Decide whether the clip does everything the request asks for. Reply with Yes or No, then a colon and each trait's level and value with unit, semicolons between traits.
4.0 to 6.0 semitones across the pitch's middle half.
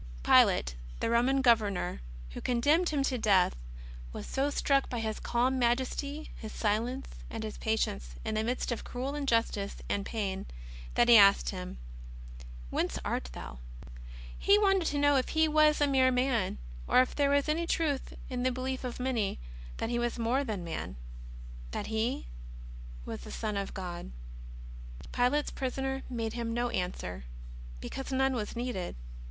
Yes: average, 4.6 semitones